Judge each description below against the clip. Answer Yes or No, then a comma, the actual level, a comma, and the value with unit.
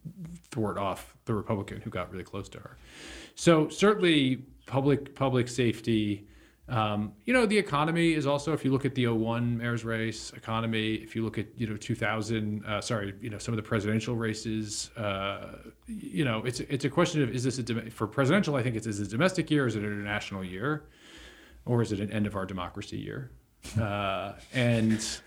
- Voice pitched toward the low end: Yes, low, 115 Hz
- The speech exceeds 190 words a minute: Yes, average, 200 wpm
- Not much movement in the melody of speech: No, average, 4.6 semitones